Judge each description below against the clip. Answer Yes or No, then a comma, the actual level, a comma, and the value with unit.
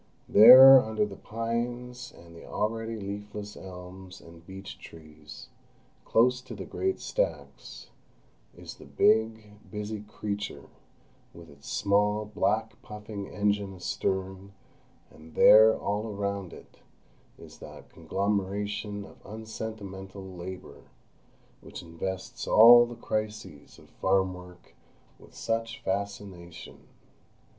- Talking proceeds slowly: Yes, slow, 110 wpm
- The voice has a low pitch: Yes, low, 100 Hz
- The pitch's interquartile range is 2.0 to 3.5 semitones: Yes, narrow, 2.6 semitones